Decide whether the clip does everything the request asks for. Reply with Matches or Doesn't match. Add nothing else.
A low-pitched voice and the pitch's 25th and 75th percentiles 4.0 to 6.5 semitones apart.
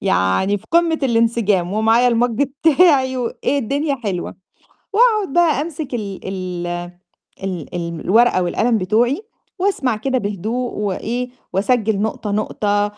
Doesn't match